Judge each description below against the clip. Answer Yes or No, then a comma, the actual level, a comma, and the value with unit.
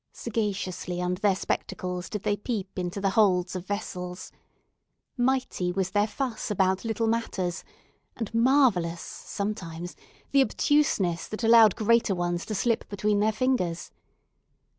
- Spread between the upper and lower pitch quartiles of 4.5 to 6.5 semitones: No, average, 4.0 semitones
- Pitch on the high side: Yes, high, 200 Hz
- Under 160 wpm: Yes, slow, 135 wpm